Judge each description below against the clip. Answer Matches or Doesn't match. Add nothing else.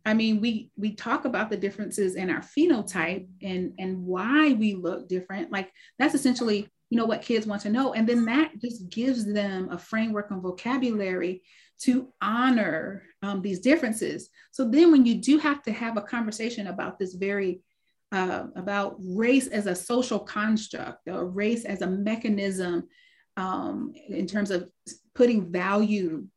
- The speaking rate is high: Doesn't match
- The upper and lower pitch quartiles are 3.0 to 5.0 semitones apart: Matches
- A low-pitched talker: Doesn't match